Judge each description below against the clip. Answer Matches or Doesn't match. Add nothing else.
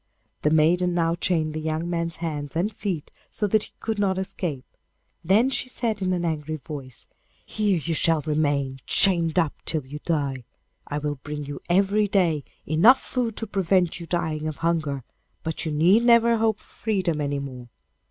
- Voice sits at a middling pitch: Matches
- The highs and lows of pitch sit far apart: Doesn't match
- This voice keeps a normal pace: Matches